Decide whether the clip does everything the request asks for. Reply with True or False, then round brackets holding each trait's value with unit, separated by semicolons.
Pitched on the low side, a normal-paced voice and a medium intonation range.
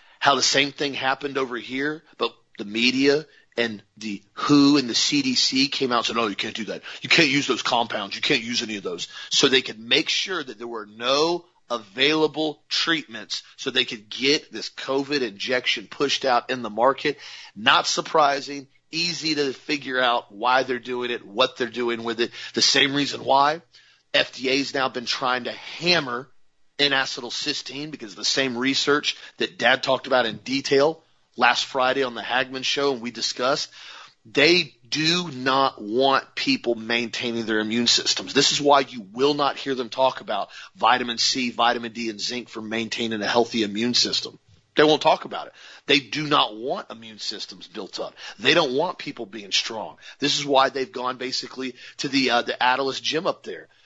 True (130 Hz; 190 wpm; 3.1 semitones)